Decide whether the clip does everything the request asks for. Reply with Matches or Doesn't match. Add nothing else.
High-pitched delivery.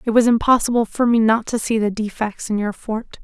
Matches